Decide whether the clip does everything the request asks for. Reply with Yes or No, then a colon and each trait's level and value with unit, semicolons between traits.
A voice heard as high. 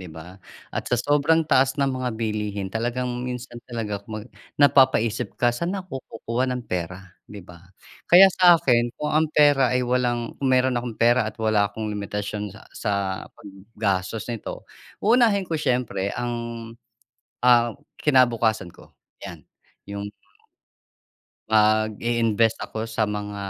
No: low, 115 Hz